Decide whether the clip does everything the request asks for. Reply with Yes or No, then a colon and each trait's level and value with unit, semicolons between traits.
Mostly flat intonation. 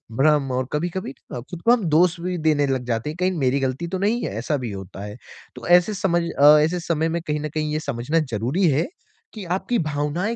No: average, 4.9 semitones